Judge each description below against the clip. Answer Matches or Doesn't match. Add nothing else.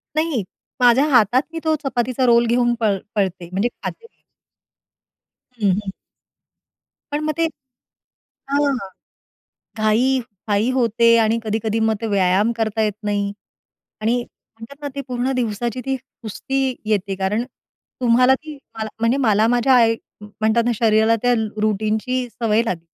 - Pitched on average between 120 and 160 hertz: Doesn't match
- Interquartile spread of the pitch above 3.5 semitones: Doesn't match